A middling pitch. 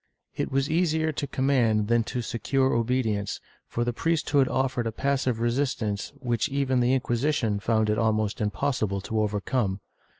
No: low, 120 Hz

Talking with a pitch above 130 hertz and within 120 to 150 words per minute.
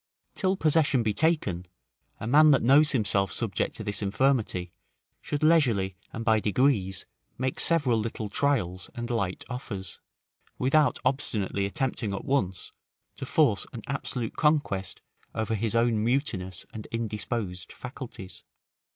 No: low, 115 Hz; slow, 135 wpm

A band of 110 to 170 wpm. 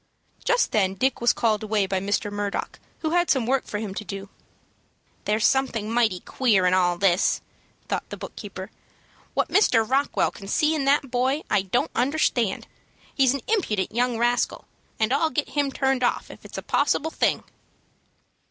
No: average, 180 wpm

